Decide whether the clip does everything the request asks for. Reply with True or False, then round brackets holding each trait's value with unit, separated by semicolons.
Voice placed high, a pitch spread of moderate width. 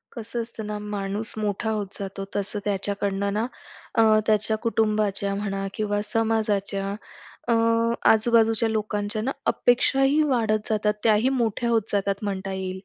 False (210 Hz; 1.9 semitones)